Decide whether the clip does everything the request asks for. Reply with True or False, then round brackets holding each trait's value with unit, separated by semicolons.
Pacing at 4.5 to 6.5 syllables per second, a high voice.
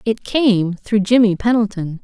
False (4.2 syllables/s; 210 Hz)